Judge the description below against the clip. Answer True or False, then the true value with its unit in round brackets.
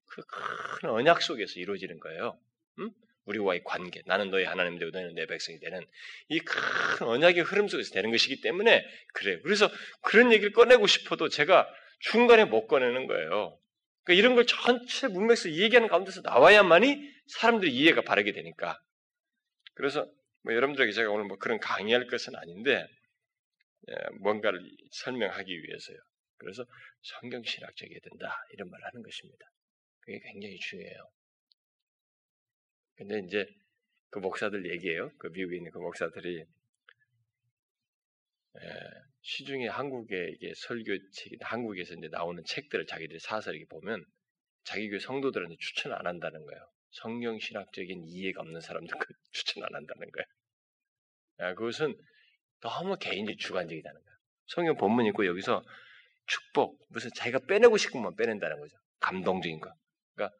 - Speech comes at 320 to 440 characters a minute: True (340 characters per minute)